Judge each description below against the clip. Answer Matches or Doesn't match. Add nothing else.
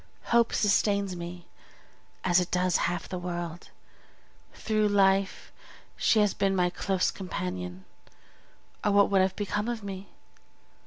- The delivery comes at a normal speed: Doesn't match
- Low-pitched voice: Doesn't match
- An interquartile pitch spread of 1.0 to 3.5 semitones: Matches